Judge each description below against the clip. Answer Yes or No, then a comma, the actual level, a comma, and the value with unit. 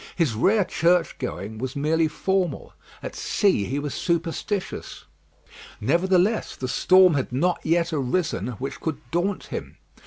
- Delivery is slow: Yes, slow, 130 wpm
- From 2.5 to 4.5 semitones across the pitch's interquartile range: No, average, 5.3 semitones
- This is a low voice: No, medium, 165 Hz